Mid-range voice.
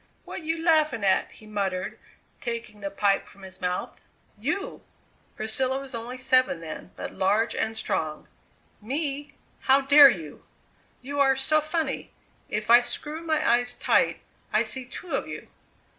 No: high, 245 Hz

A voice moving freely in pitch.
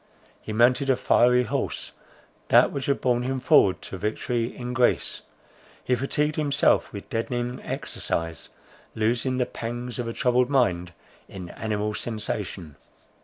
No: average, 2.9 semitones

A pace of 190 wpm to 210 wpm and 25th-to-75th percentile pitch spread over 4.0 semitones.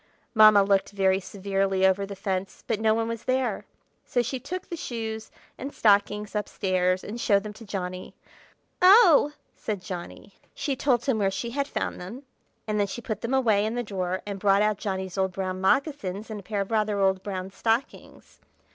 No: average, 195 wpm; average, 3.2 semitones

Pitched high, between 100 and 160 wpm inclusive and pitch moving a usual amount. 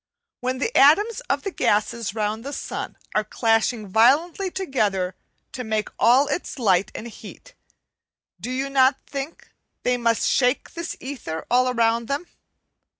Yes: very high, 250 Hz; average, 150 wpm; average, 4.2 semitones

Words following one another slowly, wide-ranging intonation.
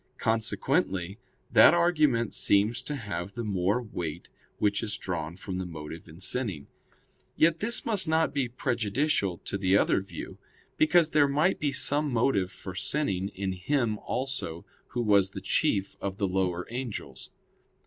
No: average, 155 wpm; wide, 6.7 semitones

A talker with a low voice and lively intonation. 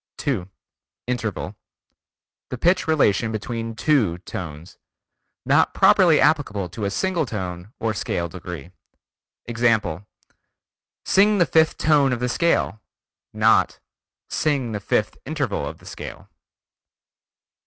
Yes: low, 115 Hz; wide, 7.1 semitones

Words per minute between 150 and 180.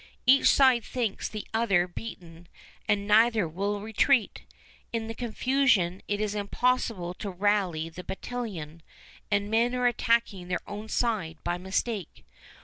No: average, 140 wpm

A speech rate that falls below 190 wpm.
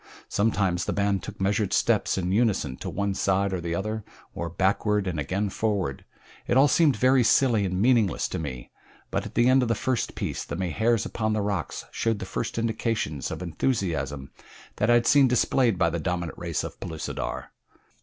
No: average, 195 wpm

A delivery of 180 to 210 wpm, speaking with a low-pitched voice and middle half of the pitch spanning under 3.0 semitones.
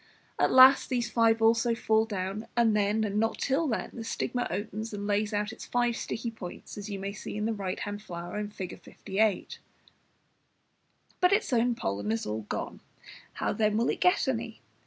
No: average, 190 wpm; high, 215 Hz; narrow, 2.4 semitones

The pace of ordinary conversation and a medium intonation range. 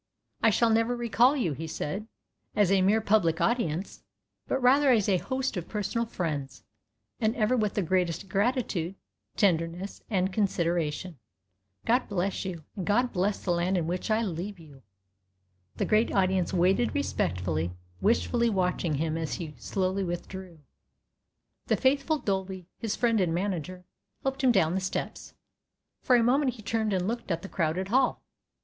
Yes: average, 160 wpm; average, 4.8 semitones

